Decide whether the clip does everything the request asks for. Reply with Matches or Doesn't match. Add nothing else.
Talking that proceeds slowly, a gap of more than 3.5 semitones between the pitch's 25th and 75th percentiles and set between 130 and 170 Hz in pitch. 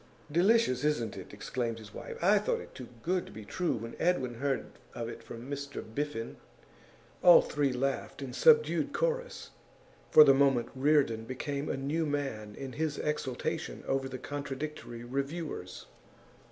Doesn't match